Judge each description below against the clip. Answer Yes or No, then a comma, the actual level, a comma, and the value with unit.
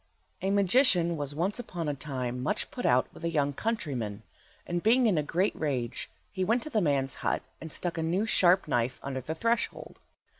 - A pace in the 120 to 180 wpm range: No, average, 200 wpm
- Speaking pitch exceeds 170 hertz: No, medium, 165 Hz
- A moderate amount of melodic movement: No, wide, 6.3 semitones